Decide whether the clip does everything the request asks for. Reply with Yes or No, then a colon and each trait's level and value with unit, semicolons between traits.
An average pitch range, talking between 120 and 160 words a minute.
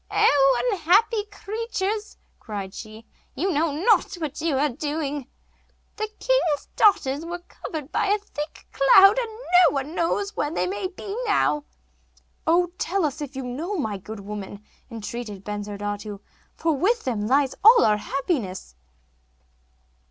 No: wide, 8.4 semitones; average, 145 wpm